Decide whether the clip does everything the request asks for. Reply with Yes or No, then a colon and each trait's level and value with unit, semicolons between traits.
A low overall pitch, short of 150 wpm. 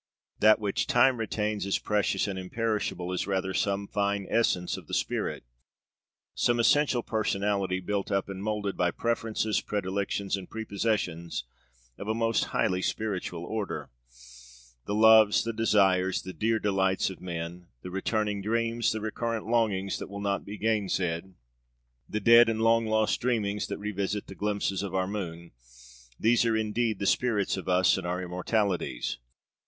No: low, 100 Hz; average, 155 wpm